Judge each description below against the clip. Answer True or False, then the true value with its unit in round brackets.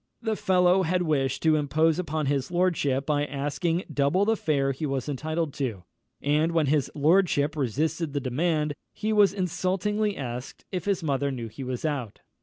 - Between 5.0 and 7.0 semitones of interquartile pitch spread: False (4.3 semitones)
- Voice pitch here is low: False (155 Hz)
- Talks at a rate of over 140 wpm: True (175 wpm)